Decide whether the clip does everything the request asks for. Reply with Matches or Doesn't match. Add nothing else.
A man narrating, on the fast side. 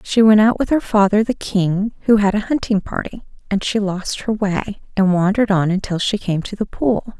Doesn't match